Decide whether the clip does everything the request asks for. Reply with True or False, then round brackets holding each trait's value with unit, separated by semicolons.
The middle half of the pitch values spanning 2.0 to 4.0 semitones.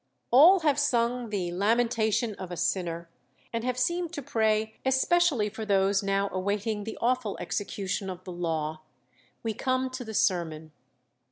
False (4.8 semitones)